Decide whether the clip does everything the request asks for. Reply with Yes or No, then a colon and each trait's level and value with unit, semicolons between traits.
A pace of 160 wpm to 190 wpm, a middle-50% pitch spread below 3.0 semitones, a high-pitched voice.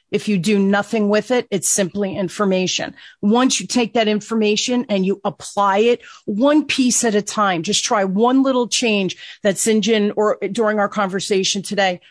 Yes: average, 180 wpm; narrow, 2.6 semitones; high, 210 Hz